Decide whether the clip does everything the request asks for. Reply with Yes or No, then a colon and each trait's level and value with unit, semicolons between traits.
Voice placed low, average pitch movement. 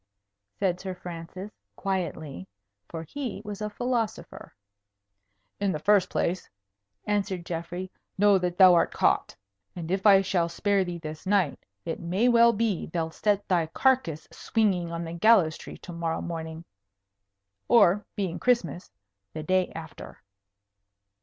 No: medium, 185 Hz; average, 3.5 semitones